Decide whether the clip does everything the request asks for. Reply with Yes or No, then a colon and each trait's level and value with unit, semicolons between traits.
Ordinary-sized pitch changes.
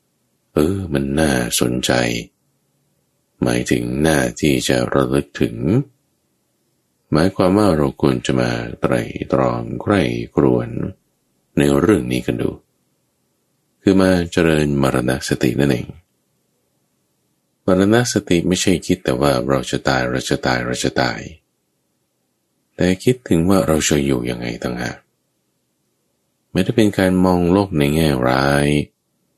No: wide, 6.5 semitones